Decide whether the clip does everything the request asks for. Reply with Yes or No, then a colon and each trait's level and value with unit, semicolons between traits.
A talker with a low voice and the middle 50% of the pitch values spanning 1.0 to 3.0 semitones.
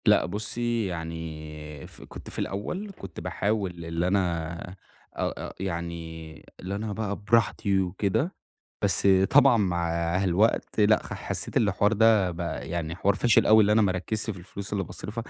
No: very low, 95 Hz; average, 4.1 semitones